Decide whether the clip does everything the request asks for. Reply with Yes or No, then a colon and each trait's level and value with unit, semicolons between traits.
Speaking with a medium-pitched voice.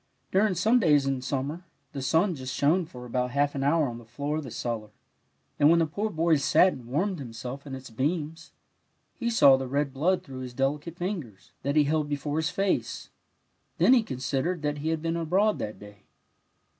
Yes: medium, 145 Hz